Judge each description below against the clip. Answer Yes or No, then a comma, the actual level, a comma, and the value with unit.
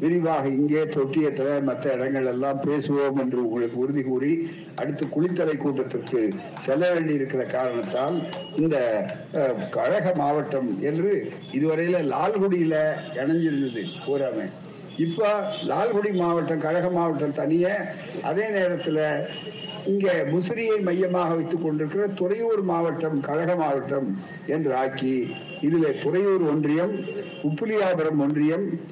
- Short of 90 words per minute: No, average, 100 wpm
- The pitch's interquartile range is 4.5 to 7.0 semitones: No, average, 3.9 semitones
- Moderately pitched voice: Yes, medium, 160 Hz